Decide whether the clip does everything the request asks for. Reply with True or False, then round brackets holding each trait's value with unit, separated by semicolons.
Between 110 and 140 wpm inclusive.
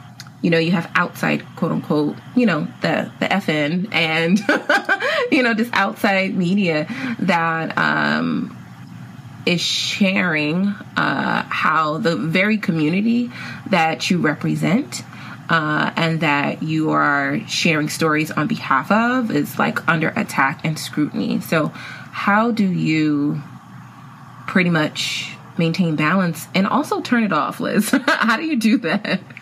True (135 wpm)